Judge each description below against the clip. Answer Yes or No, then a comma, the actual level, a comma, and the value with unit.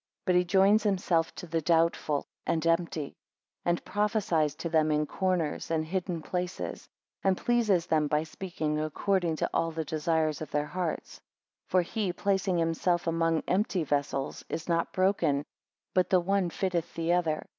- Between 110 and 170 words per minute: Yes, average, 165 wpm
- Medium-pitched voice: Yes, medium, 170 Hz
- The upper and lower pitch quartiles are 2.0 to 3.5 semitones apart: Yes, average, 2.8 semitones